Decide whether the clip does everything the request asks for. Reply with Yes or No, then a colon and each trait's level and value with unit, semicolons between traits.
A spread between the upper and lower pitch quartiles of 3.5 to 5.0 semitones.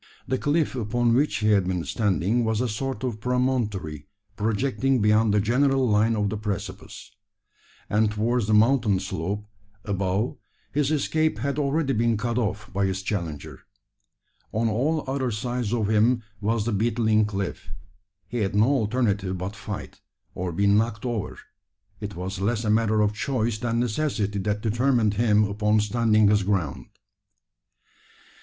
No: average, 2.9 semitones